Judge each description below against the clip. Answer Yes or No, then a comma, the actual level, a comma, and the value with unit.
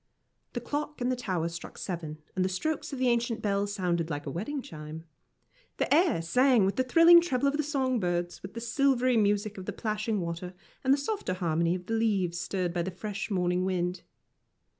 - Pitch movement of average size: No, wide, 6.3 semitones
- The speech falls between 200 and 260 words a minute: Yes, fast, 205 wpm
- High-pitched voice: Yes, high, 205 Hz